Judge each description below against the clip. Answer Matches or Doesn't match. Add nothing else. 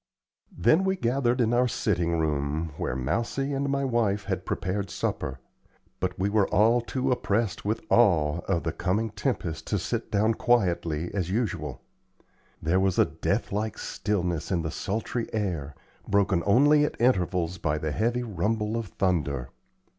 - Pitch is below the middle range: Matches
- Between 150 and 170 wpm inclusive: Matches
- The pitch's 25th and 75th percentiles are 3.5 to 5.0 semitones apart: Doesn't match